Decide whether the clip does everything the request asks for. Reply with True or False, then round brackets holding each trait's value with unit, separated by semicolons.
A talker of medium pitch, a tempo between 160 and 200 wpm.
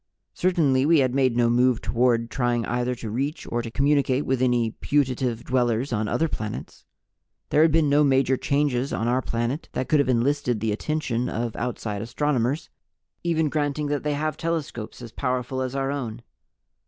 False (130 Hz; 180 wpm)